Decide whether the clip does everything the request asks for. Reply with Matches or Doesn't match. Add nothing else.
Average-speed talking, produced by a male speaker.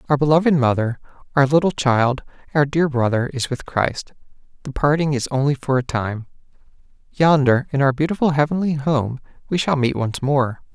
Matches